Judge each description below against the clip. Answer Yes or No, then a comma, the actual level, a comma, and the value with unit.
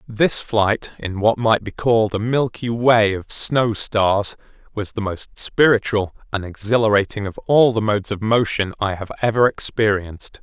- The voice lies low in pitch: Yes, low, 110 Hz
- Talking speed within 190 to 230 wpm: No, average, 165 wpm